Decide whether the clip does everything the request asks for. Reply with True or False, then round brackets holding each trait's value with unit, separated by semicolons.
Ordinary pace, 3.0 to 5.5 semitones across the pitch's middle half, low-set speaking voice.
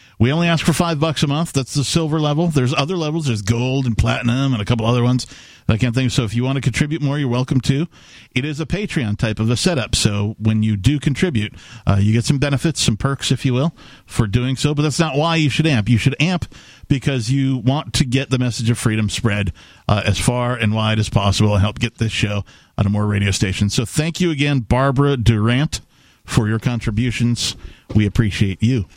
False (230 wpm; 4.6 semitones; 125 Hz)